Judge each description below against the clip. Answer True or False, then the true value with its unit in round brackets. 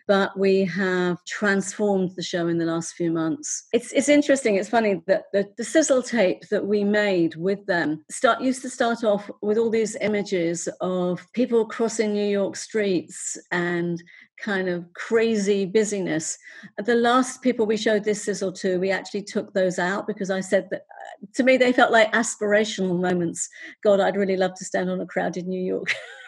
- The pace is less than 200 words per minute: True (185 wpm)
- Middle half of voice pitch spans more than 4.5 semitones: False (3.5 semitones)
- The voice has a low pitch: False (200 Hz)